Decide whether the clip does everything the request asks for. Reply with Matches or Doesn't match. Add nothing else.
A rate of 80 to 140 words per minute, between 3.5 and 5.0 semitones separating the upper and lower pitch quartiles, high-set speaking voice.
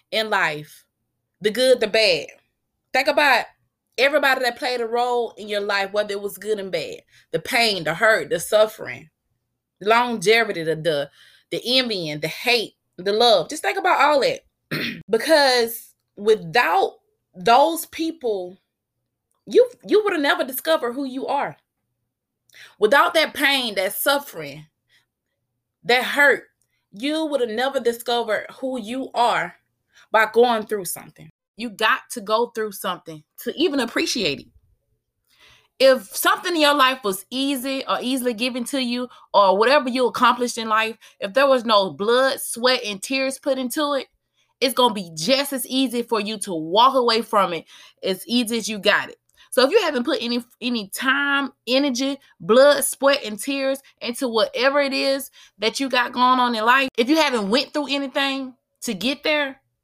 Doesn't match